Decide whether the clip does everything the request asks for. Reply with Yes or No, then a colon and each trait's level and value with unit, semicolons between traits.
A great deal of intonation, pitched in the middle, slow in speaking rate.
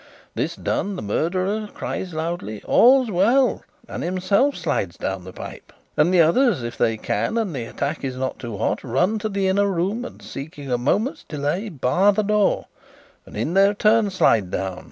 No: wide, 7.8 semitones; medium, 180 Hz; average, 185 wpm